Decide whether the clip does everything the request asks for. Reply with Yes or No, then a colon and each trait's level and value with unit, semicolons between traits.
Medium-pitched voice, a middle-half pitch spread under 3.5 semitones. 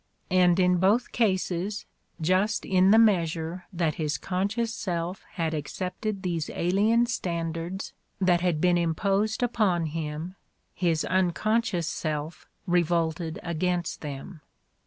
Yes: medium, 180 Hz; average, 2.9 semitones